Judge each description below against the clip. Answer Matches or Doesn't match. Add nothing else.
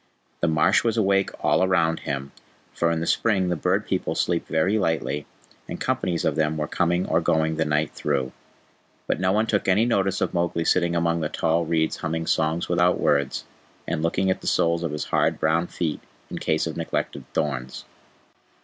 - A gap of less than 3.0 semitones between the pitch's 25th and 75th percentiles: Matches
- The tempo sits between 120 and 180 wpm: Doesn't match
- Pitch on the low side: Matches